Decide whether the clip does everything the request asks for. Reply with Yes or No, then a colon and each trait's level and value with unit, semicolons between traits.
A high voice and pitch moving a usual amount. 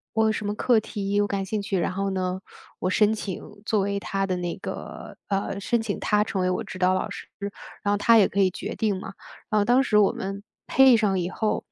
No: high, 200 Hz; narrow, 2.0 semitones